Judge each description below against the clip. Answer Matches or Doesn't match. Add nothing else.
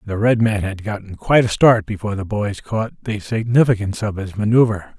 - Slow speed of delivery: Doesn't match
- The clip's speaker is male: Matches